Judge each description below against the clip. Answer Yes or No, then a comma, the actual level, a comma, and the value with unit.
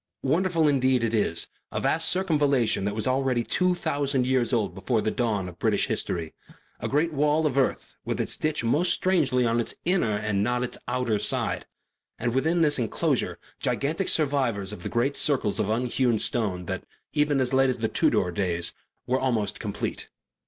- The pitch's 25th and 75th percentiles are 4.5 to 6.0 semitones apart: Yes, average, 5.1 semitones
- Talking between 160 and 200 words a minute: Yes, average, 180 wpm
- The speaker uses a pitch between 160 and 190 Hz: No, low, 125 Hz